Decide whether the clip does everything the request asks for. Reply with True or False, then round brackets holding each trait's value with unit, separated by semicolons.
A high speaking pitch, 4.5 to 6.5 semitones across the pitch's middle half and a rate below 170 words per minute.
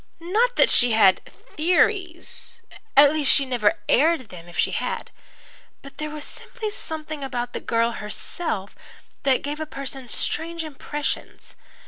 True (295 Hz; 5.2 semitones; 145 wpm)